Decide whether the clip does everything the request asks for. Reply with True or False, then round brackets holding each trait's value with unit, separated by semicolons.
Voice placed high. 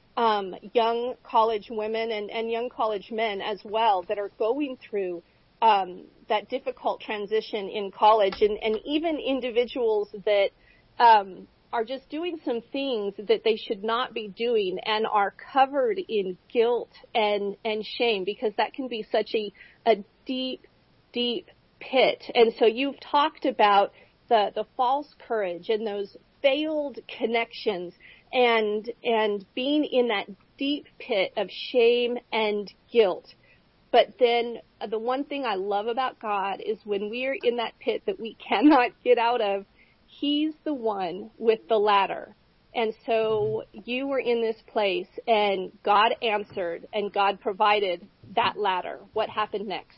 True (225 Hz)